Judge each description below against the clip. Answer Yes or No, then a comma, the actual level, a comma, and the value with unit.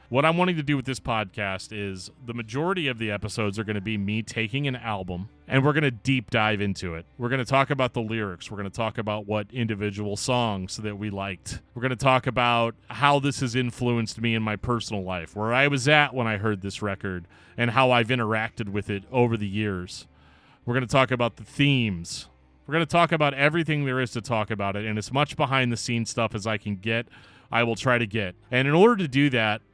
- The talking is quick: Yes, fast, 245 wpm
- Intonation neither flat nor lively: Yes, average, 3.9 semitones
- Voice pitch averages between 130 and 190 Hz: No, low, 115 Hz